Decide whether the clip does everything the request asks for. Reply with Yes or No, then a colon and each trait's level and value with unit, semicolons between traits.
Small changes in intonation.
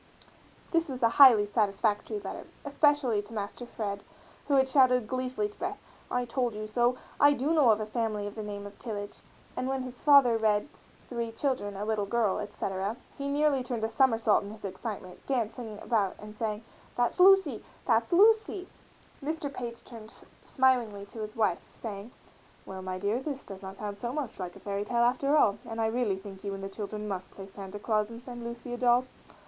No: average, 3.8 semitones